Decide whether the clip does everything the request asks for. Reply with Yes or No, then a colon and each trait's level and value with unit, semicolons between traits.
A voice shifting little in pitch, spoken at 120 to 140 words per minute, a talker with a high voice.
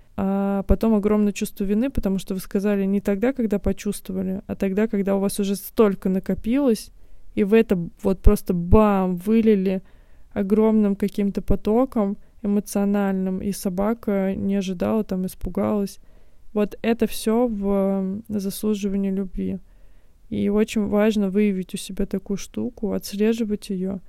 Yes: narrow, 1.5 semitones; average, 135 wpm; high, 200 Hz